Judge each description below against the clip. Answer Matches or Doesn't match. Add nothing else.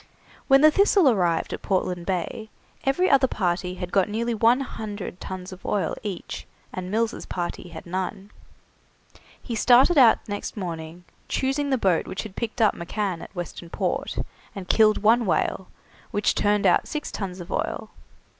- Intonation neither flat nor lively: Matches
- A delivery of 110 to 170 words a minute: Matches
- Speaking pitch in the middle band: Doesn't match